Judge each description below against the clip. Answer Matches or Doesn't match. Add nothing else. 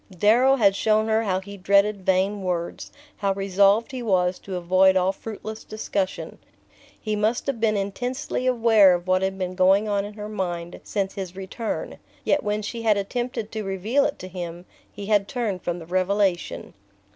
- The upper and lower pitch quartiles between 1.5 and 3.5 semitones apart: Matches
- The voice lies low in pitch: Doesn't match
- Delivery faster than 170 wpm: Matches